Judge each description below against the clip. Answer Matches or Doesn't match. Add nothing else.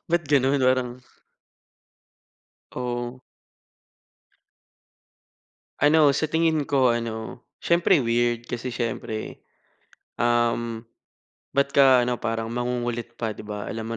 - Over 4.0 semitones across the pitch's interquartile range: Doesn't match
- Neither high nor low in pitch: Doesn't match